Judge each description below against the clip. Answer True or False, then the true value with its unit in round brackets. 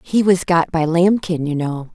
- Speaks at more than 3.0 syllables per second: True (4.4 syllables/s)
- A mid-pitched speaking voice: True (170 Hz)